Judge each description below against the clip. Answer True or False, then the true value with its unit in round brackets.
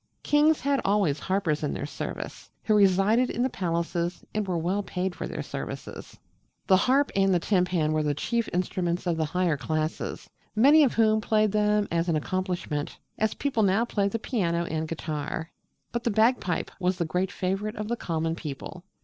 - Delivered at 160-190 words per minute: True (185 wpm)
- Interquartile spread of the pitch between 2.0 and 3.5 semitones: False (4.4 semitones)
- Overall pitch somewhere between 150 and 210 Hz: True (185 Hz)